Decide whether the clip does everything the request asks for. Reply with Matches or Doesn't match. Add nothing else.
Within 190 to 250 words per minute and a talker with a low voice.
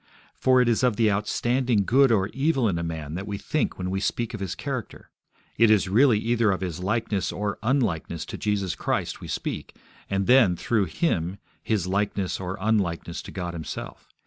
Matches